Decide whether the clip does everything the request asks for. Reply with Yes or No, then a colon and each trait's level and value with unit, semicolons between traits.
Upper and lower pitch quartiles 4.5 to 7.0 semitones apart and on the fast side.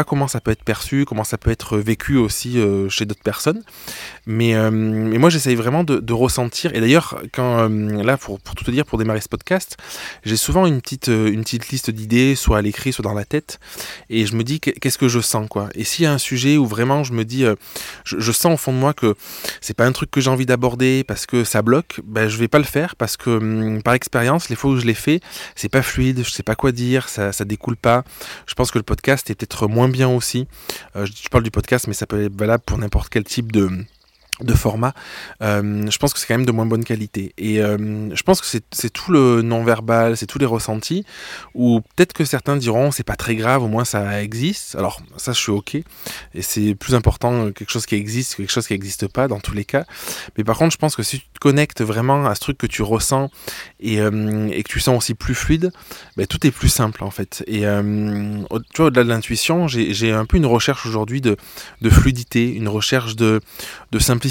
No: average, 3.5 semitones; fast, 245 wpm